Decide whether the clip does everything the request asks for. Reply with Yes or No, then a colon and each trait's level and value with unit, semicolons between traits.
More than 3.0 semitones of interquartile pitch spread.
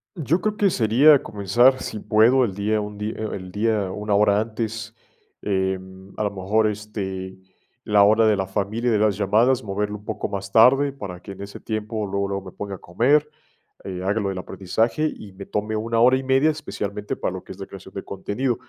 No: average, 2.7 semitones